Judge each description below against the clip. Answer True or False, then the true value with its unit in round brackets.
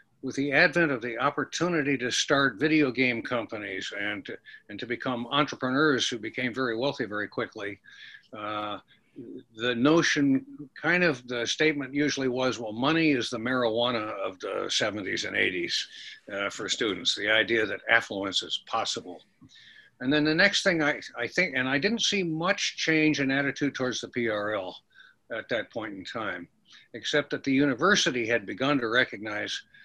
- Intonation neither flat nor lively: False (5.8 semitones)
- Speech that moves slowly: False (165 wpm)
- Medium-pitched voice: True (145 Hz)